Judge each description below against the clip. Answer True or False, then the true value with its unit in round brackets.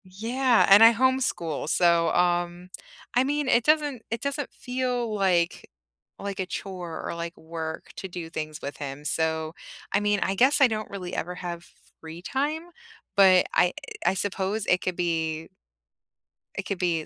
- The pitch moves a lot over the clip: True (5.7 semitones)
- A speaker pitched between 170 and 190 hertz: True (185 Hz)